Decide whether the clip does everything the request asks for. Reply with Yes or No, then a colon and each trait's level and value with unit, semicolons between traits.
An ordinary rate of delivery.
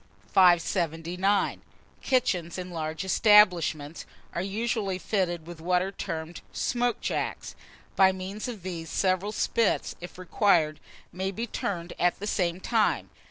No: slow, 130 wpm